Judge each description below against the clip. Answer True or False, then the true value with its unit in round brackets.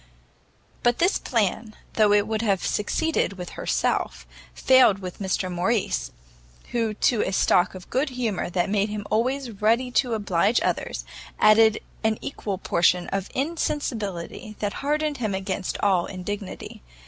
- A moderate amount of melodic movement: True (4.0 semitones)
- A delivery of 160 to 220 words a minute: False (145 wpm)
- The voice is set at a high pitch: True (210 Hz)